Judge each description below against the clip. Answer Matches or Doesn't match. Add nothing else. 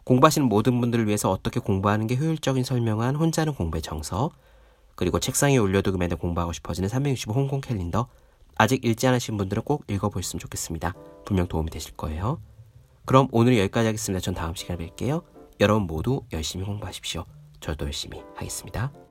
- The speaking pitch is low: Matches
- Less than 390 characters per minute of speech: Doesn't match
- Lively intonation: Matches